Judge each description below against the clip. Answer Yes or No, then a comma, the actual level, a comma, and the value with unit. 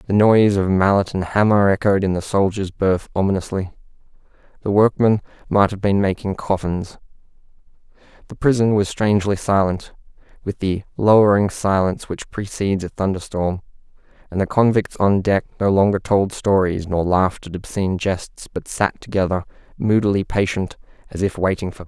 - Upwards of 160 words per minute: No, average, 155 wpm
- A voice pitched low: Yes, low, 100 Hz